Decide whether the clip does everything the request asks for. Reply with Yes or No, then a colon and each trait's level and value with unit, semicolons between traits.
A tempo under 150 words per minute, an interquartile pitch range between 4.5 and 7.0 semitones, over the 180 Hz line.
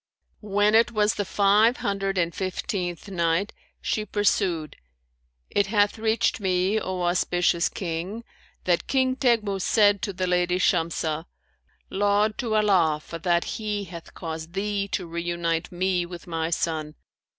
No: average, 140 wpm; average, 3.2 semitones; high, 190 Hz